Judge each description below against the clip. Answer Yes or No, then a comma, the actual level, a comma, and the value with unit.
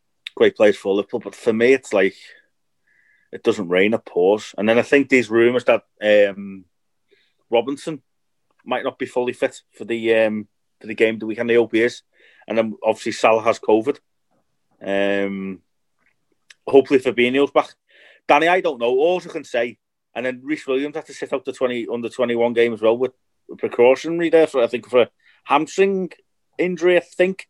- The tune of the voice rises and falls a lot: Yes, wide, 5.7 semitones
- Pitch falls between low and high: No, low, 125 Hz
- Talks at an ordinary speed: Yes, average, 185 wpm